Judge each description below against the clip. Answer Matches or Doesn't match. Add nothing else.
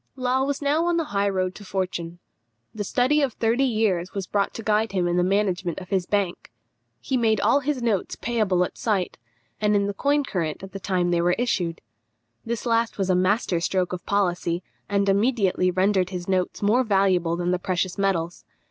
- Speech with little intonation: Doesn't match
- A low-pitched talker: Doesn't match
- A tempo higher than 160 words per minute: Matches